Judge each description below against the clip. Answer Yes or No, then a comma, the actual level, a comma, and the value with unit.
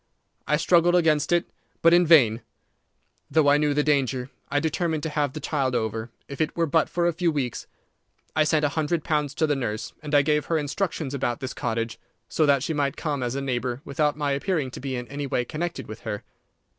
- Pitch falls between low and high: Yes, medium, 145 Hz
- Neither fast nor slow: No, fast, 220 wpm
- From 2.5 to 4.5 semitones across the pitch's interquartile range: Yes, average, 3.2 semitones